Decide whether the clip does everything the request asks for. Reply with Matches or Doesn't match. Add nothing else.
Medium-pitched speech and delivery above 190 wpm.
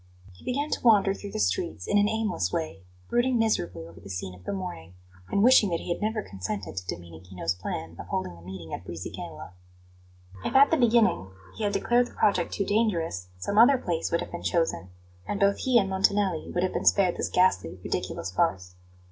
Matches